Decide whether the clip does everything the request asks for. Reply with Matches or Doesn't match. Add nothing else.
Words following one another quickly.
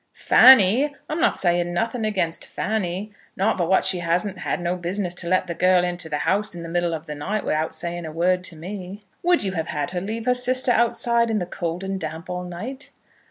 Matches